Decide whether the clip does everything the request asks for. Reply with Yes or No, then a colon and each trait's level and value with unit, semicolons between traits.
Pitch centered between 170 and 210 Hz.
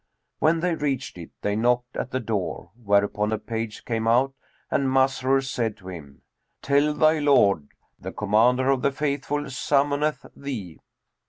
No: low, 125 Hz